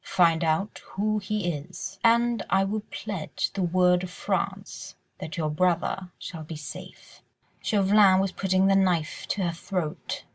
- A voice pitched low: No, medium, 185 Hz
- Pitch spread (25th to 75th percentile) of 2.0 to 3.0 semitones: Yes, average, 2.7 semitones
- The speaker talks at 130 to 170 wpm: Yes, average, 155 wpm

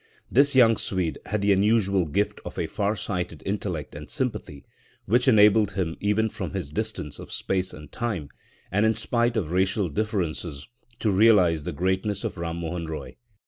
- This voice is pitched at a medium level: No, low, 100 Hz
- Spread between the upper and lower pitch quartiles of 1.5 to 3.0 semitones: No, average, 4.3 semitones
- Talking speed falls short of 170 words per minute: No, average, 175 wpm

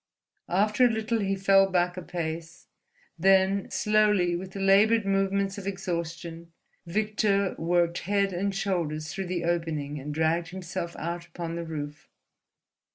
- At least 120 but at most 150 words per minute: Yes, average, 145 wpm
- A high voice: No, medium, 180 Hz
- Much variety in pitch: No, average, 2.8 semitones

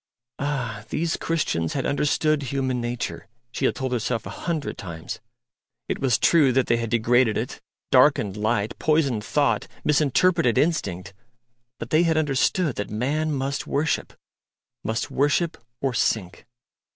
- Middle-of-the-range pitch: No, low, 130 Hz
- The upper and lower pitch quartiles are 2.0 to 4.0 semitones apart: No, average, 5.0 semitones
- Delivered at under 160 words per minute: Yes, average, 140 wpm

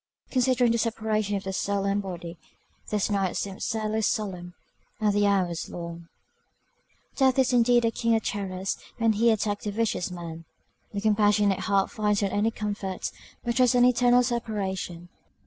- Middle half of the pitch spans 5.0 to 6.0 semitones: No, average, 2.9 semitones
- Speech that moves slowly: No, average, 165 wpm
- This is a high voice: Yes, high, 205 Hz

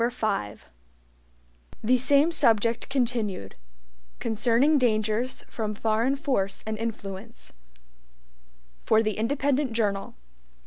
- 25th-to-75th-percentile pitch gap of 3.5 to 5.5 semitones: No, average, 3.1 semitones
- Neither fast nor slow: No, slow, 90 wpm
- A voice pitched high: Yes, high, 230 Hz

